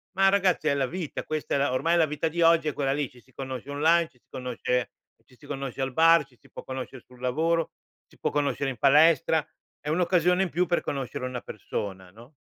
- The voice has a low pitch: No, medium, 145 Hz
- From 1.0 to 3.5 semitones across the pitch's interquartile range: No, average, 4.3 semitones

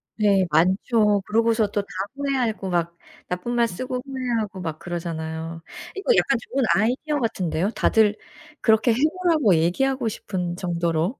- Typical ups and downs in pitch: No, wide, 5.7 semitones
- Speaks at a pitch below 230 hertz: Yes, high, 210 Hz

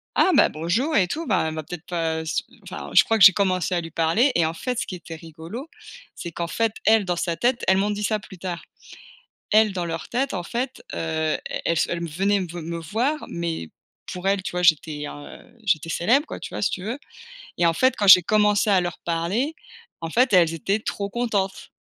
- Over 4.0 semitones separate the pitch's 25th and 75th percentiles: Yes, average, 4.4 semitones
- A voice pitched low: No, medium, 185 Hz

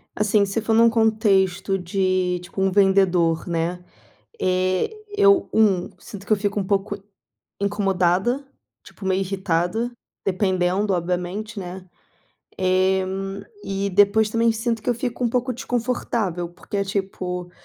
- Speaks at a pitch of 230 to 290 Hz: No, high, 195 Hz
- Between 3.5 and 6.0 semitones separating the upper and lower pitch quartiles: No, average, 3.0 semitones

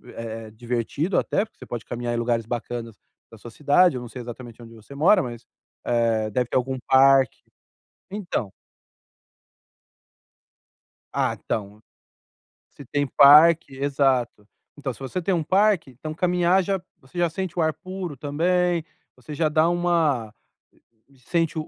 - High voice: No, medium, 140 Hz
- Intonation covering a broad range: Yes, wide, 6.0 semitones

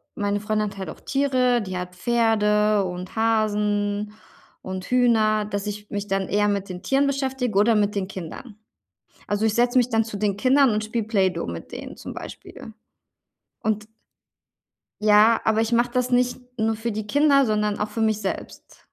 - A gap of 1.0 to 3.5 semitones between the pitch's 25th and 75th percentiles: Yes, narrow, 2.4 semitones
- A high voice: Yes, high, 215 Hz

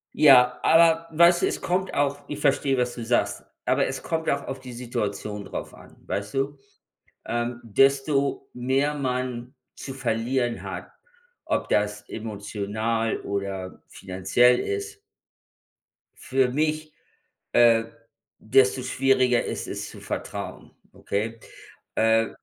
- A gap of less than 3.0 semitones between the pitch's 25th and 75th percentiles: No, average, 3.6 semitones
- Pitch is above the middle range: No, low, 125 Hz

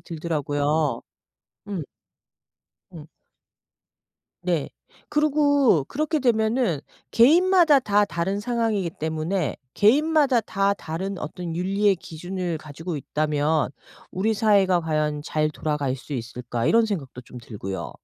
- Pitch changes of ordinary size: No, wide, 6.4 semitones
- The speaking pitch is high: No, medium, 180 Hz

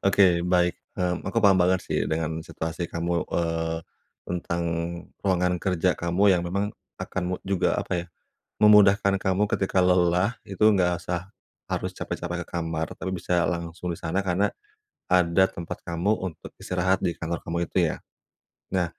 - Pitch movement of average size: No, narrow, 1.7 semitones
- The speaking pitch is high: No, very low, 90 Hz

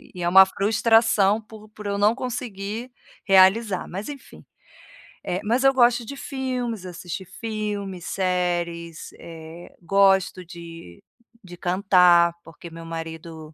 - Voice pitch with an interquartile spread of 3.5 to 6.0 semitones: Yes, average, 4.2 semitones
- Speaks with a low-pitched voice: No, high, 190 Hz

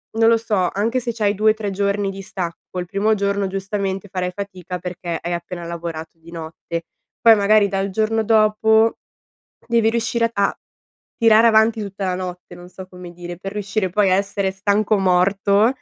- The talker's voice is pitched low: No, high, 200 Hz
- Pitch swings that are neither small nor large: Yes, average, 3.0 semitones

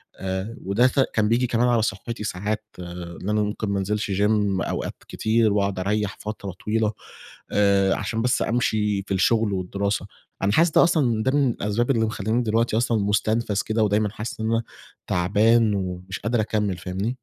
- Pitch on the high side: No, low, 105 Hz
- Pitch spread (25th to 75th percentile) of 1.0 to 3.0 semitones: Yes, narrow, 2.5 semitones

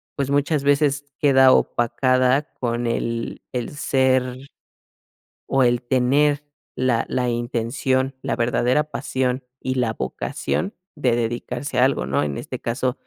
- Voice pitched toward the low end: Yes, low, 130 Hz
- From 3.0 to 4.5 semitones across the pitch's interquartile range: No, narrow, 2.5 semitones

